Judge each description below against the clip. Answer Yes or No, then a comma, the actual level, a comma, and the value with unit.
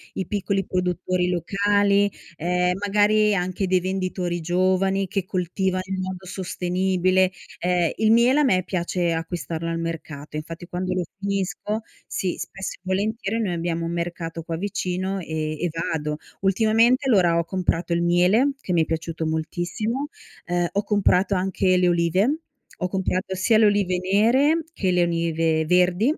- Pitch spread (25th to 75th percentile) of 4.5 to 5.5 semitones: No, narrow, 2.5 semitones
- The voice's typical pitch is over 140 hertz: Yes, medium, 185 Hz